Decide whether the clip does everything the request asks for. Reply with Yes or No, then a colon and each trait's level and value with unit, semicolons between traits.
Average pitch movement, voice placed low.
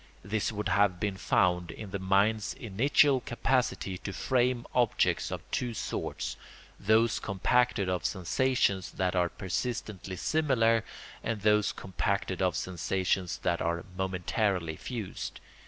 Yes: average, 3.7 semitones; low, 100 Hz